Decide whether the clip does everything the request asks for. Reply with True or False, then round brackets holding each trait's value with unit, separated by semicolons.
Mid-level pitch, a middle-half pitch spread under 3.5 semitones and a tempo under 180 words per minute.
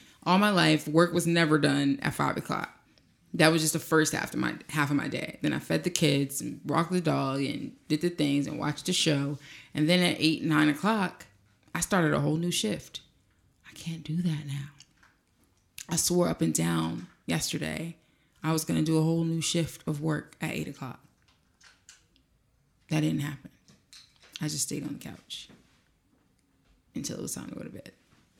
False (155 Hz; 2.7 semitones; 195 wpm)